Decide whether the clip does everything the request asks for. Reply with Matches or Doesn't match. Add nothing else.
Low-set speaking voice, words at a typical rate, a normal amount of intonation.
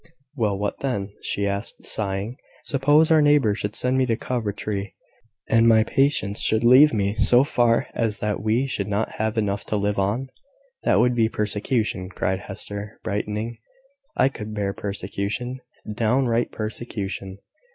Matches